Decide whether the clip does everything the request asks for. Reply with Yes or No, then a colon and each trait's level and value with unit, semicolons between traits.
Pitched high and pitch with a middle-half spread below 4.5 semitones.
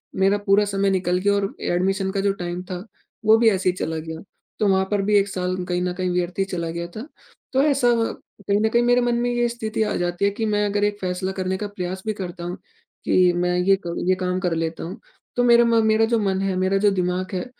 Yes: high, 195 Hz; narrow, 2.5 semitones